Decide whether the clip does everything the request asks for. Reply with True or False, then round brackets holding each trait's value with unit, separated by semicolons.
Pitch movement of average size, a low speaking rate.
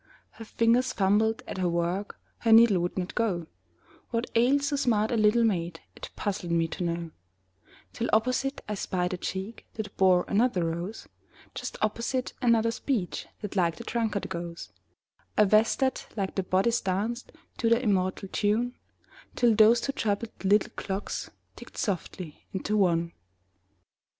False (4.0 semitones; 155 wpm)